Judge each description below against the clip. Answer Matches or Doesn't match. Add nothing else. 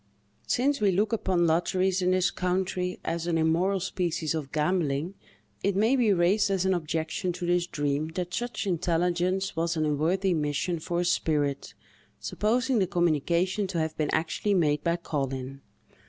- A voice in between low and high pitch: Matches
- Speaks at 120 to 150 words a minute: Doesn't match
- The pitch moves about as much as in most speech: Matches